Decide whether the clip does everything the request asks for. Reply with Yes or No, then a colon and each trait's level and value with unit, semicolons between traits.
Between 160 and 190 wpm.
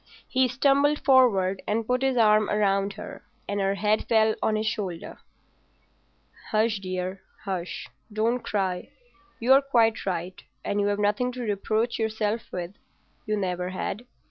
No: average, 140 wpm